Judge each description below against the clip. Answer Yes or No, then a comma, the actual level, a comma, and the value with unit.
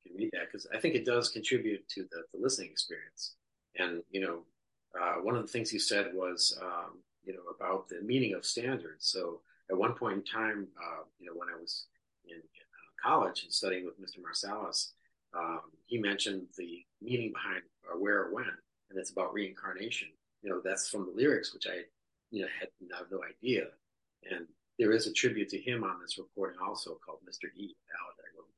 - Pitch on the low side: Yes, low, 110 Hz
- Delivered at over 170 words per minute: Yes, average, 200 wpm